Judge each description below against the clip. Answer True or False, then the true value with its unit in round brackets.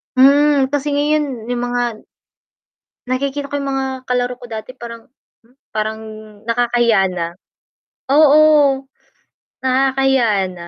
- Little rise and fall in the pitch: False (3.2 semitones)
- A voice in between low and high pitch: False (255 Hz)